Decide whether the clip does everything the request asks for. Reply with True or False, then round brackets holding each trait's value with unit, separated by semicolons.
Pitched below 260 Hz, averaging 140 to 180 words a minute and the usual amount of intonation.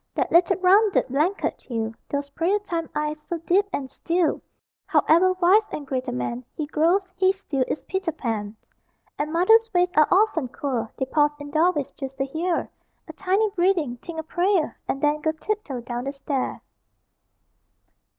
False (320 Hz; 170 wpm; 5.0 semitones)